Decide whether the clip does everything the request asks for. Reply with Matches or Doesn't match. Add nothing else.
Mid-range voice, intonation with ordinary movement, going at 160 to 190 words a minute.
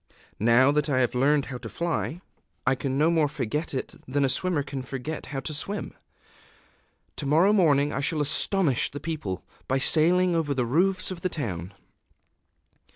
Matches